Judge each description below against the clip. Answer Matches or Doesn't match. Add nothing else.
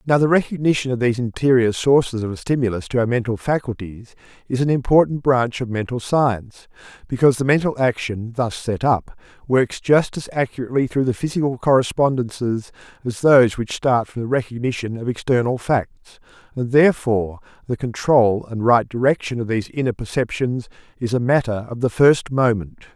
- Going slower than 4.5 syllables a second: Doesn't match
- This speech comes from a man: Matches